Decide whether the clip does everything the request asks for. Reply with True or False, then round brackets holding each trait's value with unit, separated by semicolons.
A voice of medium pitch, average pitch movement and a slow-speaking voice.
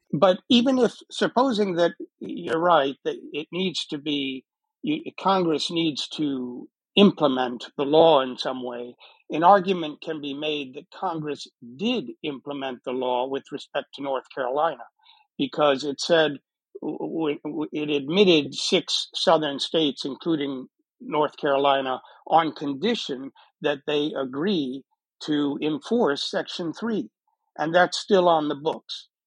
False (155 Hz; 5.7 semitones; 130 wpm)